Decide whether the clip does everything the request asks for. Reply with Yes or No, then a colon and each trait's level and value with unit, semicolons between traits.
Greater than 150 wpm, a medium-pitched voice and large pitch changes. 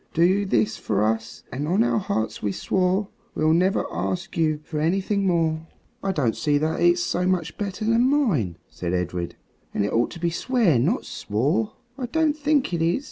Yes: average, 190 wpm; medium, 170 Hz; wide, 8.7 semitones